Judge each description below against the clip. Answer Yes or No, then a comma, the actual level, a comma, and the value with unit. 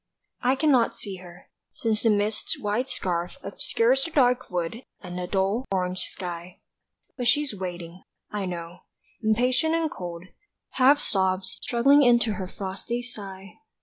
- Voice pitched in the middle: No, high, 205 Hz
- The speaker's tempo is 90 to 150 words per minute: Yes, average, 145 wpm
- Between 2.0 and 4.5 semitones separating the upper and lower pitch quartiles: No, average, 5.2 semitones